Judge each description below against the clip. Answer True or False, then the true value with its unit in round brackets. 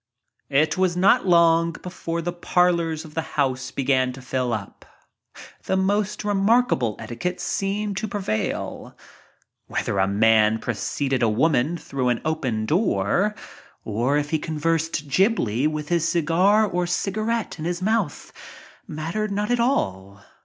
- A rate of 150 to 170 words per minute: False (135 wpm)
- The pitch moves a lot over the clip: True (6.5 semitones)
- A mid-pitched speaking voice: True (165 Hz)